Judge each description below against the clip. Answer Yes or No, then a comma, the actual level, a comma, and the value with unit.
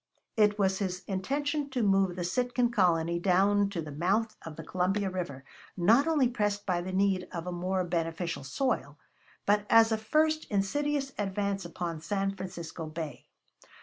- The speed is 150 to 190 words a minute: Yes, average, 165 wpm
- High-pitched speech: Yes, high, 195 Hz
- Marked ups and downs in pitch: No, average, 4.0 semitones